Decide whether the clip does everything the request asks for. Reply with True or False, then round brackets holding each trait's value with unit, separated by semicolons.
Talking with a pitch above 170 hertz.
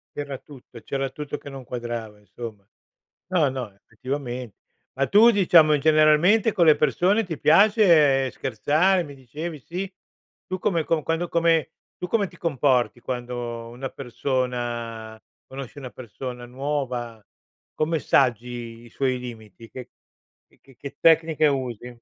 False (135 Hz)